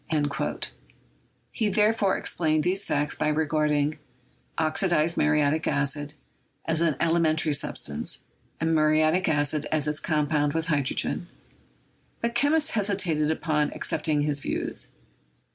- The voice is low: No, medium, 155 Hz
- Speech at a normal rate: No, slow, 125 wpm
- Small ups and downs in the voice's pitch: Yes, narrow, 2.2 semitones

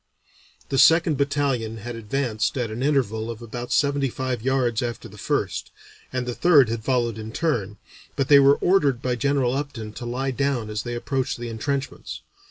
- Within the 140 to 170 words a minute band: No, average, 180 wpm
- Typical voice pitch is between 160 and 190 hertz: No, low, 125 Hz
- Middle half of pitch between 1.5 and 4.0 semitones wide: Yes, average, 3.4 semitones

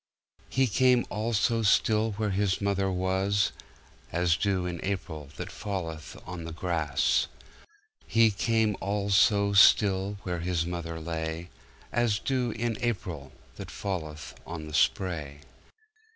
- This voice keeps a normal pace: No, slow, 110 wpm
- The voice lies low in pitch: Yes, very low, 95 Hz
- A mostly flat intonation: No, average, 3.8 semitones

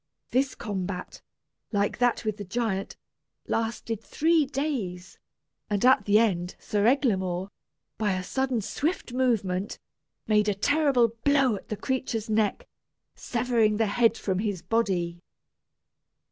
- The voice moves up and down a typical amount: Yes, average, 4.1 semitones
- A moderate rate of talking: No, slow, 130 wpm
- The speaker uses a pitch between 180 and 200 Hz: No, high, 220 Hz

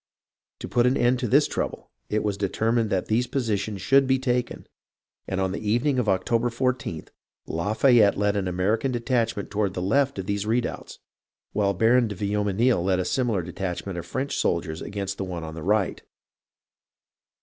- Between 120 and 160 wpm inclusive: No, average, 180 wpm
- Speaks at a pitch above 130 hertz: No, low, 105 Hz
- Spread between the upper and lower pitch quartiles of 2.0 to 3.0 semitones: No, average, 4.1 semitones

